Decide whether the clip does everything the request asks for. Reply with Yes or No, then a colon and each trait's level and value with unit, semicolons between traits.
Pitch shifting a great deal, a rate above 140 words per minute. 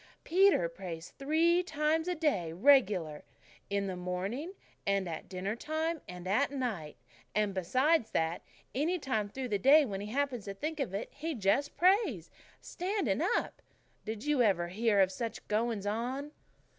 Yes: wide, 7.5 semitones; average, 160 wpm